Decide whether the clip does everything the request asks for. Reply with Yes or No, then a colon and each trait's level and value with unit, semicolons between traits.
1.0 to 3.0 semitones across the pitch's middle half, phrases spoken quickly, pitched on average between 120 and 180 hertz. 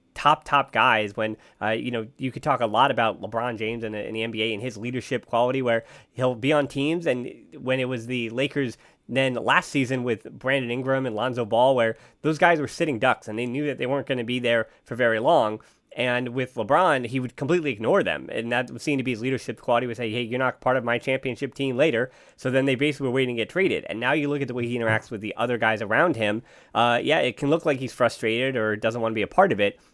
Yes: narrow, 2.6 semitones; fast, 265 wpm; low, 125 Hz